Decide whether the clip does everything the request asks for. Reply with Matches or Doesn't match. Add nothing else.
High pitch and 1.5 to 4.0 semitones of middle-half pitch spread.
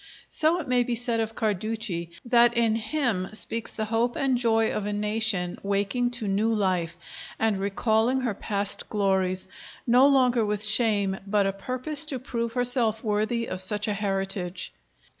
Matches